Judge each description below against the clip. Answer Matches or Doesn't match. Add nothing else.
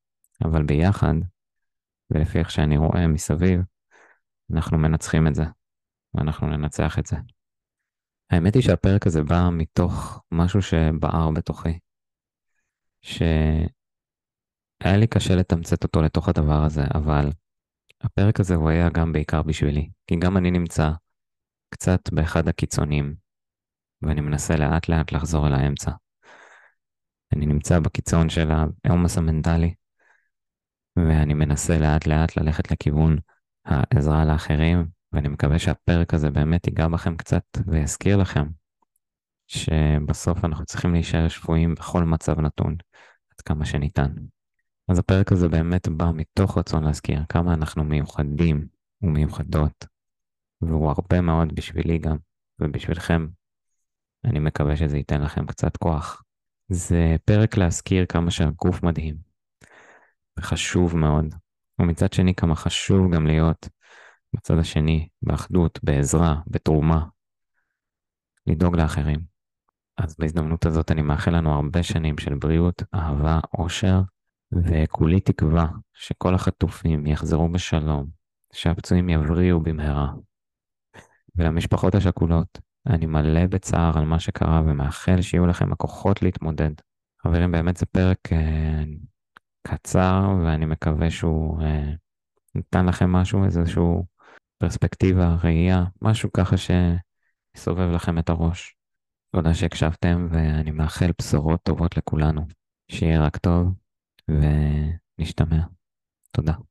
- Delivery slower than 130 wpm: Matches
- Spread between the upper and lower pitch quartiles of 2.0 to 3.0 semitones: Matches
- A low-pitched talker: Matches